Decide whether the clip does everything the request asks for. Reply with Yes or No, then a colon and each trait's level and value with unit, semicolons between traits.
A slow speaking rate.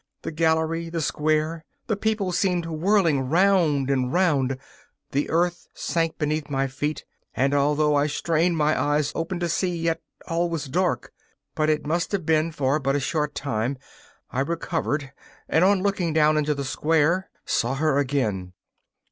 No: average, 165 wpm